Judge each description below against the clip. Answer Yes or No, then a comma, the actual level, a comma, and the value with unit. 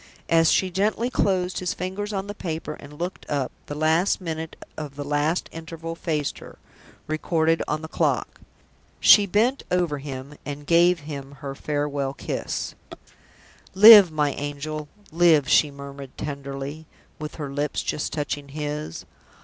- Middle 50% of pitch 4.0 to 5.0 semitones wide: No, average, 3.3 semitones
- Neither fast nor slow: Yes, average, 150 wpm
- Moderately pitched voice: Yes, medium, 155 Hz